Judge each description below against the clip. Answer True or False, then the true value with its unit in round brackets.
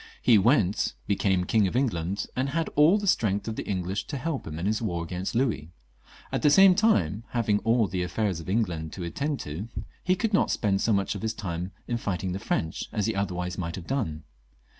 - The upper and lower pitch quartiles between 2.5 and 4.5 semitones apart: False (5.0 semitones)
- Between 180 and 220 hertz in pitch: False (100 Hz)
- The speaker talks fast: True (220 wpm)